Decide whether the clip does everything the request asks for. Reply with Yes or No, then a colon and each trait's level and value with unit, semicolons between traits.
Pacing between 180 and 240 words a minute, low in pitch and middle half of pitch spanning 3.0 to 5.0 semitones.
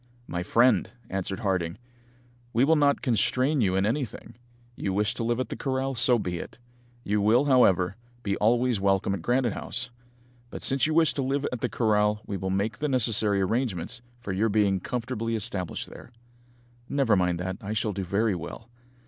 Yes: average, 185 wpm; low, 110 Hz; average, 4.5 semitones